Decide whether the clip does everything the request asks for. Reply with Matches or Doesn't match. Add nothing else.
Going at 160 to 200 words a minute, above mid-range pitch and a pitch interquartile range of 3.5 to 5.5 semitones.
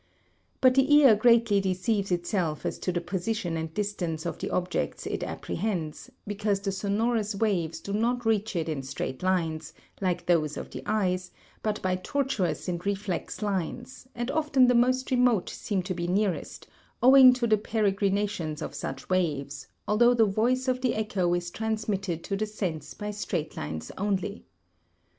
Matches